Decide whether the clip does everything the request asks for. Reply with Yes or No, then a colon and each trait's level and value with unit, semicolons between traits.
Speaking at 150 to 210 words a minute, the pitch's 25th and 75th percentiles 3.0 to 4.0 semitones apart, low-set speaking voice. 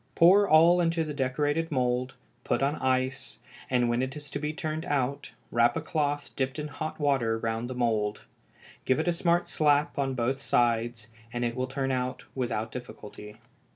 Yes: average, 185 wpm; average, 3.7 semitones; low, 130 Hz